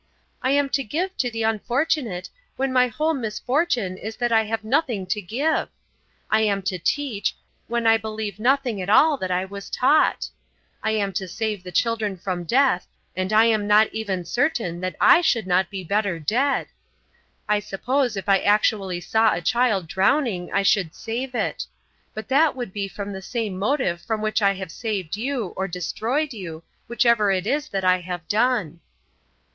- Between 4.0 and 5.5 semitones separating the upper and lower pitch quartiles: Yes, average, 4.5 semitones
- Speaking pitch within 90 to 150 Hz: No, high, 215 Hz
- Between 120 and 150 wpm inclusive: No, average, 185 wpm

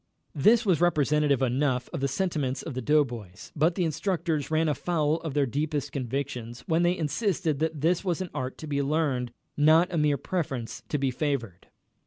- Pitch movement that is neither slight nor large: Yes, average, 3.4 semitones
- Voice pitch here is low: No, medium, 150 Hz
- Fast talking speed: No, average, 185 wpm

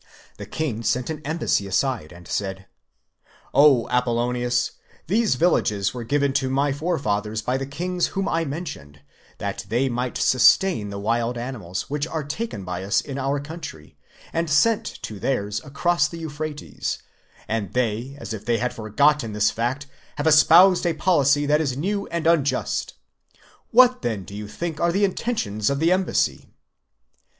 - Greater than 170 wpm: No, average, 165 wpm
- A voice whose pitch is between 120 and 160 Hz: Yes, low, 135 Hz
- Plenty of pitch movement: Yes, wide, 6.4 semitones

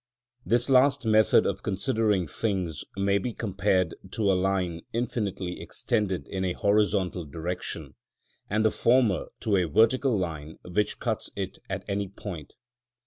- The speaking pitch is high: No, low, 100 Hz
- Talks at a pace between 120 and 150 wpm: Yes, average, 140 wpm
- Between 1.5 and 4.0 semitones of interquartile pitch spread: Yes, average, 3.4 semitones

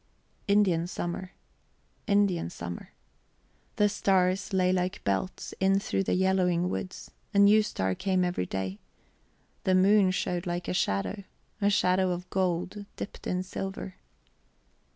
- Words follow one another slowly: Yes, slow, 130 wpm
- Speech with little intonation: Yes, narrow, 1.8 semitones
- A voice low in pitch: No, medium, 185 Hz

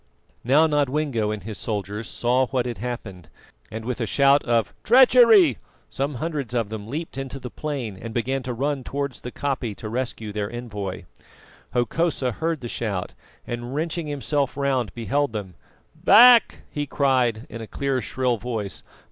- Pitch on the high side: No, low, 125 Hz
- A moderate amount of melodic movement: Yes, average, 4.2 semitones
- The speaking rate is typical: Yes, average, 165 wpm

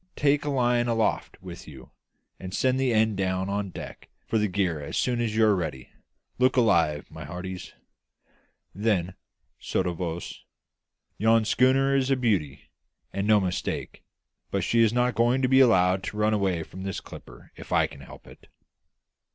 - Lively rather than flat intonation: No, average, 4.9 semitones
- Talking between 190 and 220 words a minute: No, average, 175 wpm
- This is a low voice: Yes, low, 105 Hz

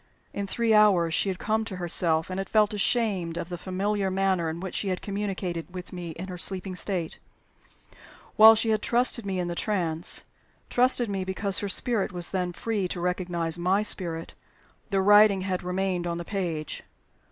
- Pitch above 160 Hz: Yes, high, 190 Hz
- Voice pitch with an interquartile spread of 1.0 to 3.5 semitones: Yes, average, 2.7 semitones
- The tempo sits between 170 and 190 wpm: Yes, average, 185 wpm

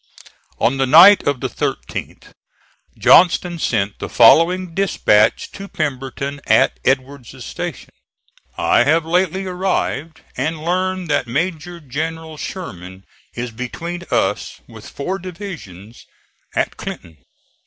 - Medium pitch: Yes, medium, 155 Hz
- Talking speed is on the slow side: Yes, slow, 115 wpm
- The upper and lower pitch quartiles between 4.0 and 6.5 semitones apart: Yes, wide, 5.6 semitones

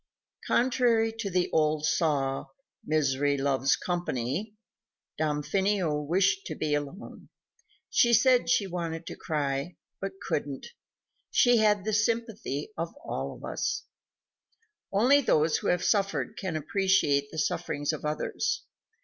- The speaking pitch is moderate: Yes, medium, 170 Hz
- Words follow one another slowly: Yes, slow, 125 wpm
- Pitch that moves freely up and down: Yes, wide, 5.7 semitones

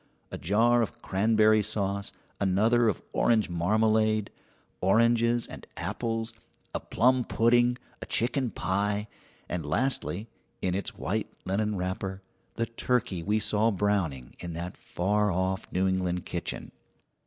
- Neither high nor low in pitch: No, low, 105 Hz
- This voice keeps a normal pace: No, slow, 130 wpm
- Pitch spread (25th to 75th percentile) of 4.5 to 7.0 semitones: No, average, 3.3 semitones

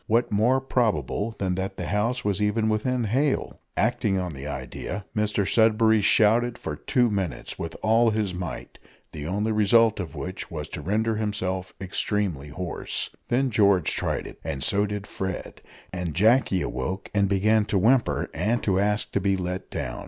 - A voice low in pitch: Yes, low, 105 Hz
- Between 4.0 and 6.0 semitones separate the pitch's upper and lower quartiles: No, average, 3.3 semitones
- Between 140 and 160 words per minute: No, average, 175 wpm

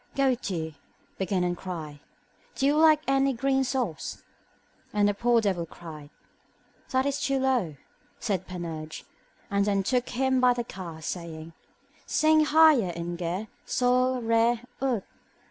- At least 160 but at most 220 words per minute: No, average, 140 wpm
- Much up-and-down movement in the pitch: Yes, wide, 7.1 semitones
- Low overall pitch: No, high, 225 Hz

